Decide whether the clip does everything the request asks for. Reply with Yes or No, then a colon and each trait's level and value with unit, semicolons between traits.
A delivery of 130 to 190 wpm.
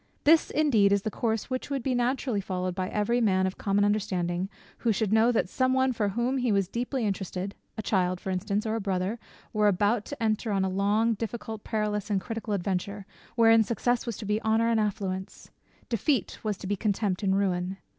No: fast, 205 wpm